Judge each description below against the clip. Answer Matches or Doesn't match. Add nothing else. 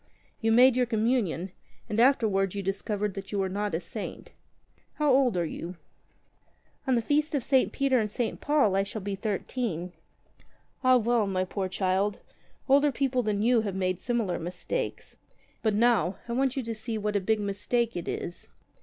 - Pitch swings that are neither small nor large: Matches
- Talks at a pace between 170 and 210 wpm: Matches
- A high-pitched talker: Matches